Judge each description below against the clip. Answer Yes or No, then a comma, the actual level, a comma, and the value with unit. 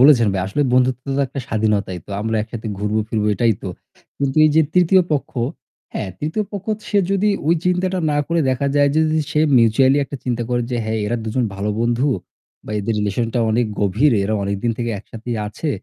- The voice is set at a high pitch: No, low, 120 Hz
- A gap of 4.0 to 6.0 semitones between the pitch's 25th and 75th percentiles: Yes, average, 5.1 semitones